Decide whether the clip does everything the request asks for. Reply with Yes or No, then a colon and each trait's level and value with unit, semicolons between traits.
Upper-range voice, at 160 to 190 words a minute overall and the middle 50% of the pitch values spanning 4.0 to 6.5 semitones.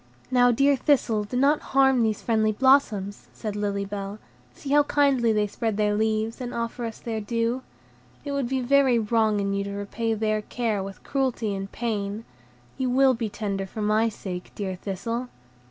No: high, 225 Hz; average, 185 wpm; average, 3.4 semitones